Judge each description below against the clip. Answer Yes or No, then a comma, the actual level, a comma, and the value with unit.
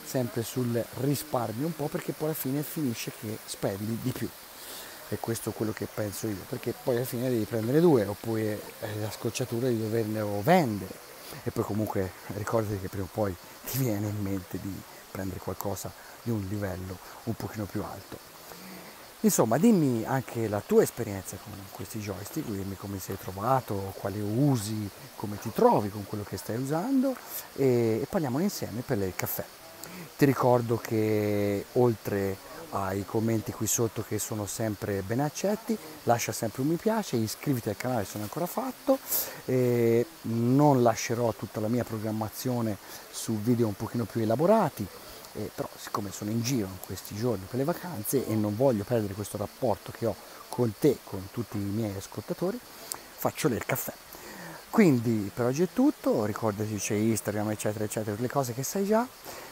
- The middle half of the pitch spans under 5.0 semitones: Yes, average, 4.1 semitones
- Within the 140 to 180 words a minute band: Yes, fast, 170 wpm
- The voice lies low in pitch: Yes, low, 115 Hz